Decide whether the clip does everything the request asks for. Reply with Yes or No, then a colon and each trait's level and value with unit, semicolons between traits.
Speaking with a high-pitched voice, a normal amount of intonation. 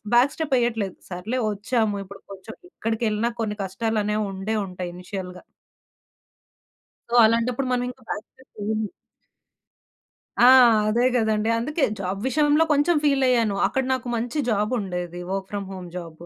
Yes: high, 220 Hz; average, 4.1 semitones